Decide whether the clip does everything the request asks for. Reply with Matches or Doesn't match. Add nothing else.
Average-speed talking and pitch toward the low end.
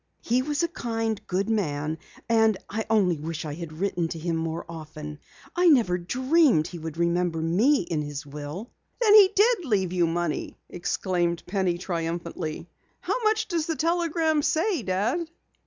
Doesn't match